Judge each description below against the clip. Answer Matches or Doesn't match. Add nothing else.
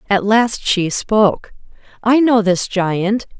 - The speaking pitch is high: Matches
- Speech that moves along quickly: Doesn't match